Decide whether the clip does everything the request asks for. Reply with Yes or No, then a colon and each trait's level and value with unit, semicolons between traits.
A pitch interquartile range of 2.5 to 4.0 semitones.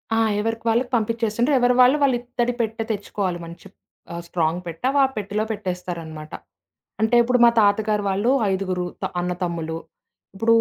No: average, 4.6 semitones